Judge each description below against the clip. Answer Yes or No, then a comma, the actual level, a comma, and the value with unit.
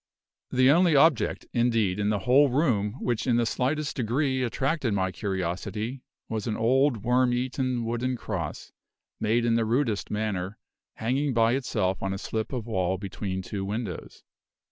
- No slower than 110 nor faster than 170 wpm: Yes, average, 160 wpm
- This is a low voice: Yes, low, 115 Hz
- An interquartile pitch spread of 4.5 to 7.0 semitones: No, average, 3.8 semitones